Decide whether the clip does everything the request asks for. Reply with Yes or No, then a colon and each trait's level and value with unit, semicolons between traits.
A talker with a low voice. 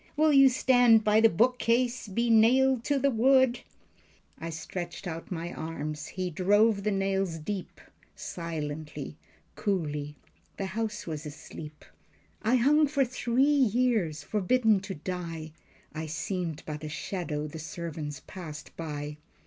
No: high, 190 Hz